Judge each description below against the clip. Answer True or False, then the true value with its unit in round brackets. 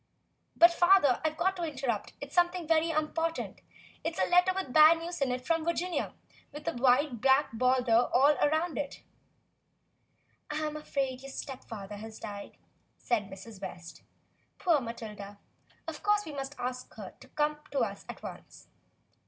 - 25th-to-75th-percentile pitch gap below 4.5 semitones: False (5.0 semitones)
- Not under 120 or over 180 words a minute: True (160 wpm)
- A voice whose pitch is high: True (285 Hz)